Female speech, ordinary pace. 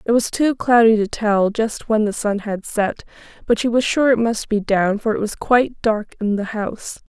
No: female; fast, 235 wpm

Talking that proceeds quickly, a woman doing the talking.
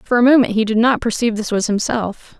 Yes: fast, 250 wpm; female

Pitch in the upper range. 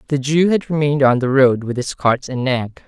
No: low, 135 Hz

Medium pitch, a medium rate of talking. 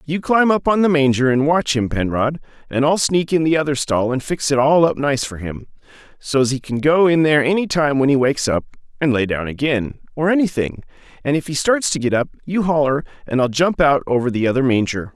No: medium, 145 Hz; fast, 240 wpm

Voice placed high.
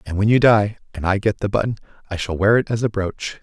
No: low, 105 Hz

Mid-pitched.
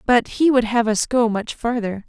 No: high, 230 Hz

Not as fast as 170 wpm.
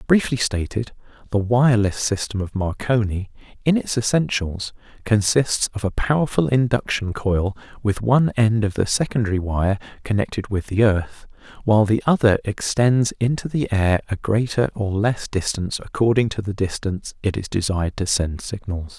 Yes: average, 155 wpm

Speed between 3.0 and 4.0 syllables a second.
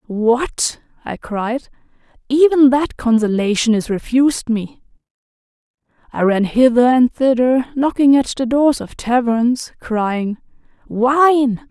Yes: 3.7 syllables/s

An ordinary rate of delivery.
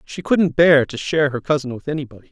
No: fast, 235 wpm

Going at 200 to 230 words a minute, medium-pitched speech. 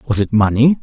No: fast, 215 wpm; low, 120 Hz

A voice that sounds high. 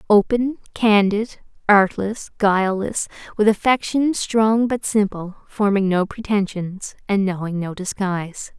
Yes: high, 205 Hz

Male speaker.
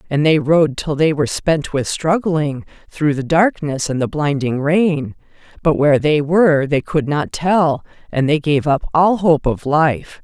No: female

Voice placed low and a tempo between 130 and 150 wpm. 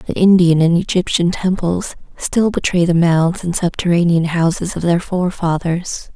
No: medium, 175 Hz; average, 145 wpm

